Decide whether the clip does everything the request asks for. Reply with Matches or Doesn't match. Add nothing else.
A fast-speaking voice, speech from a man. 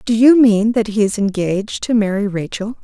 Doesn't match